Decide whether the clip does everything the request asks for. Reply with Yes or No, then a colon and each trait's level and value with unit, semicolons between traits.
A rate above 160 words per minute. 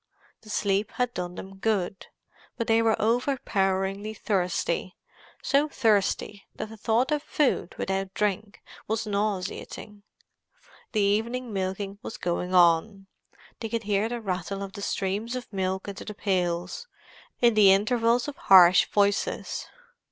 No: slow, 135 wpm